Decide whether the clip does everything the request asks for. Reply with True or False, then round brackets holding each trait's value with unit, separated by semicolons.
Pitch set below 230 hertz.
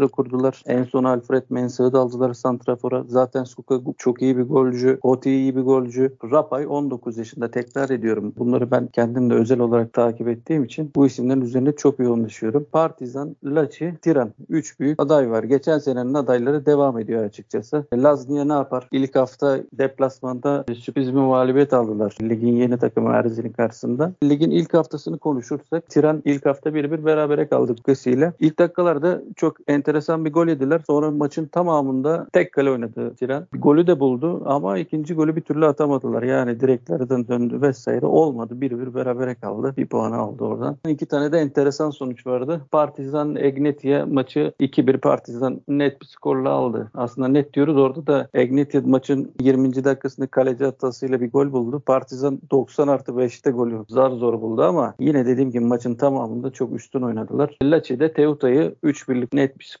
True (135 Hz)